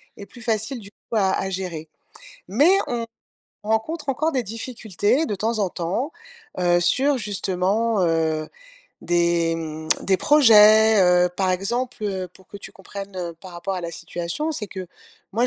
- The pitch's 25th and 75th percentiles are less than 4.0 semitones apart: No, average, 4.4 semitones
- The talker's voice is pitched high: Yes, high, 200 Hz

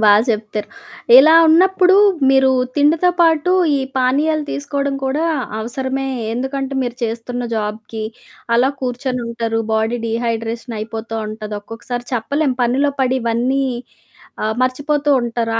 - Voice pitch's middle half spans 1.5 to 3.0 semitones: No, average, 3.8 semitones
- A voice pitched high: Yes, very high, 250 Hz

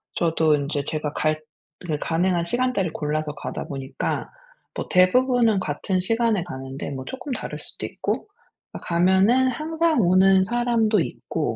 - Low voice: No, medium, 185 Hz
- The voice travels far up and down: Yes, wide, 7.4 semitones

